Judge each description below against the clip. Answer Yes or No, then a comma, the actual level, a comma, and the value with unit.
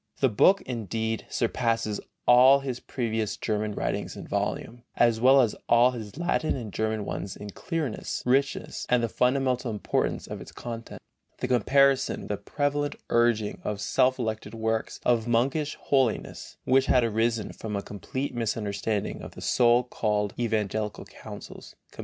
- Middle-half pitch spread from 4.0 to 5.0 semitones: No, average, 3.0 semitones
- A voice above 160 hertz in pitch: No, low, 115 Hz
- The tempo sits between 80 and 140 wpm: No, average, 155 wpm